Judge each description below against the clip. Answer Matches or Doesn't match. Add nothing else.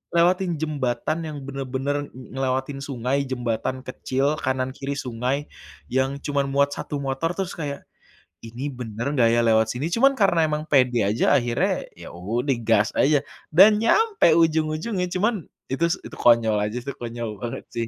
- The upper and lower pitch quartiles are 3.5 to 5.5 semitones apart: Matches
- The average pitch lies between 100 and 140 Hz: Matches